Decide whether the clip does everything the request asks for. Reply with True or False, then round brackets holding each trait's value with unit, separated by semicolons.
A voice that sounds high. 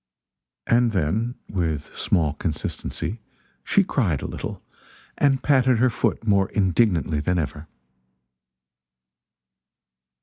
False (100 Hz)